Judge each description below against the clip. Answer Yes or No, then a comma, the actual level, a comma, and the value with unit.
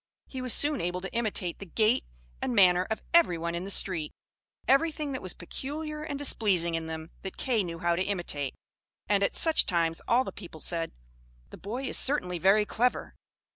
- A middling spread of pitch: No, wide, 7.0 semitones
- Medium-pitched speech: No, high, 195 Hz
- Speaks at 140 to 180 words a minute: No, average, 190 wpm